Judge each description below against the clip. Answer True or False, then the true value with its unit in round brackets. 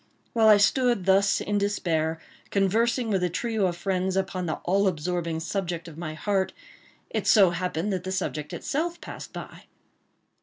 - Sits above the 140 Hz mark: True (190 Hz)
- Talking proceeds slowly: False (165 wpm)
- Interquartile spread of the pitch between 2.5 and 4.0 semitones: True (3.0 semitones)